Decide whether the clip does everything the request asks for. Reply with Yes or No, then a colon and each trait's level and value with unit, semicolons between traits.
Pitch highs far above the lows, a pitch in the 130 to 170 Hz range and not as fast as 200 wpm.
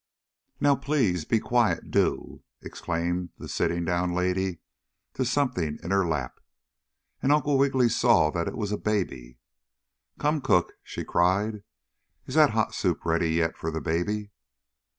No: wide, 6.3 semitones; very low, 90 Hz; average, 150 wpm